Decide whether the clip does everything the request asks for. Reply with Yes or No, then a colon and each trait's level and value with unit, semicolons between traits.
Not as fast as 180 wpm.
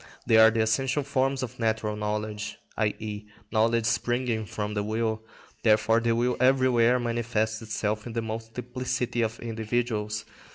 Yes: average, 140 wpm